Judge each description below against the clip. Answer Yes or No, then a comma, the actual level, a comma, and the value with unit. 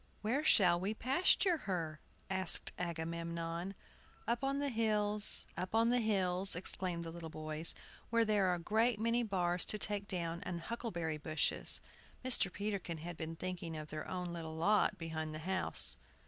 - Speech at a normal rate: Yes, average, 165 wpm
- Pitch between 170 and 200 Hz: Yes, medium, 185 Hz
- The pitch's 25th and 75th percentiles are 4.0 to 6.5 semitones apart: Yes, average, 4.3 semitones